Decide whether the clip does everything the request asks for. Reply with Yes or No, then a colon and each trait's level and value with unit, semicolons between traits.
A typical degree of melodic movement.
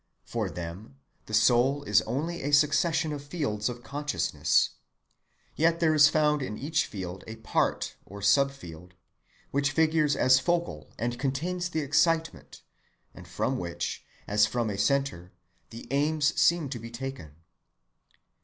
No: wide, 6.3 semitones